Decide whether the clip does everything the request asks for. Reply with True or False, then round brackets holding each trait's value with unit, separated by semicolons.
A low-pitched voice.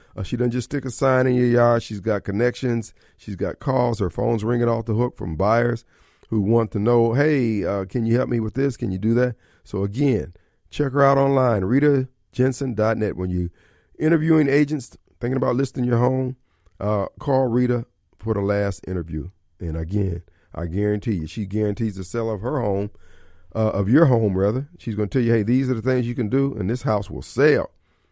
True (115 Hz)